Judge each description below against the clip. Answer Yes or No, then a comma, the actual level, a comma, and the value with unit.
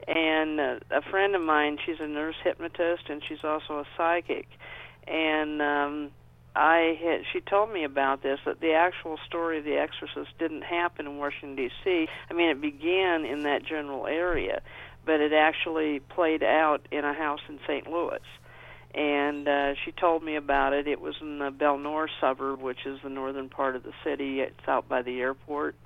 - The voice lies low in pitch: No, medium, 150 Hz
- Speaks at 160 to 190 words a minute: Yes, average, 185 wpm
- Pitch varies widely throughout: No, narrow, 2.6 semitones